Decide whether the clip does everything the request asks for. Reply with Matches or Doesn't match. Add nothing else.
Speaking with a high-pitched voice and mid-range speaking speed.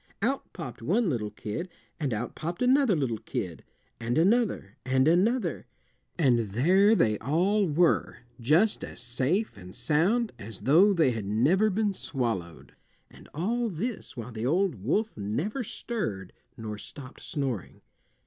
Doesn't match